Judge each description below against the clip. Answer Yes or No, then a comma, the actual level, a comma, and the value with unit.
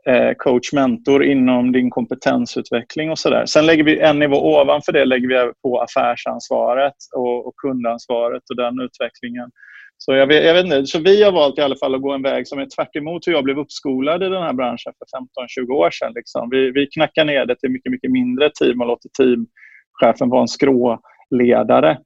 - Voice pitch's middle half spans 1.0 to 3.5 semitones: Yes, average, 3.2 semitones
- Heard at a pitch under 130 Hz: No, low, 135 Hz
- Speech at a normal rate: No, fast, 200 wpm